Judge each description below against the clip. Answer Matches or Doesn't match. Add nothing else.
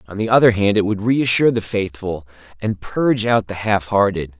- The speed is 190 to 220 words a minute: Matches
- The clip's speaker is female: Doesn't match